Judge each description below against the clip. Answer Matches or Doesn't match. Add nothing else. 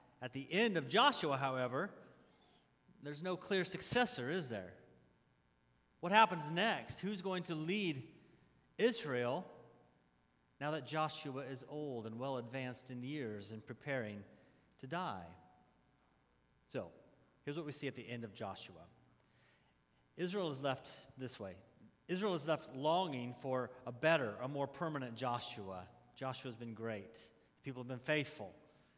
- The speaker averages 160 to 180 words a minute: Doesn't match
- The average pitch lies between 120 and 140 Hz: Matches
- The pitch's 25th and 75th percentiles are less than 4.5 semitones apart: Doesn't match